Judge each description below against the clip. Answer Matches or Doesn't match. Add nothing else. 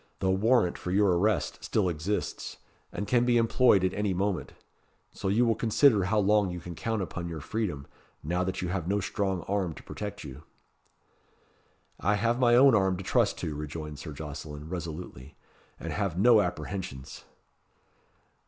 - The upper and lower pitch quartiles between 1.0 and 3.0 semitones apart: Doesn't match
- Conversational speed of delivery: Matches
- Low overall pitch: Matches